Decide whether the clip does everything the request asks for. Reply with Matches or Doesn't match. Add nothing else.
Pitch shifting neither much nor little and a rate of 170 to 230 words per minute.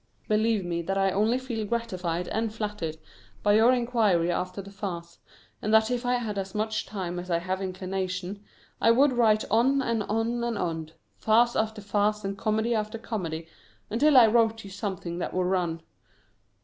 Matches